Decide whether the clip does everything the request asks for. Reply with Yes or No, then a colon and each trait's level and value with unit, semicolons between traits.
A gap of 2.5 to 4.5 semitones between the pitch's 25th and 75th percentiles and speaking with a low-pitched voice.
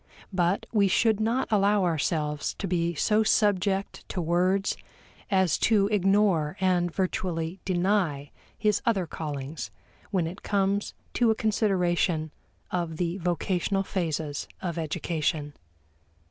No: average, 3.3 semitones; medium, 185 Hz